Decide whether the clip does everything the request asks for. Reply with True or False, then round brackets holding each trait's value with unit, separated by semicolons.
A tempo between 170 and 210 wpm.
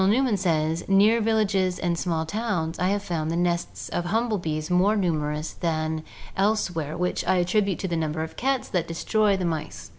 True (190 wpm)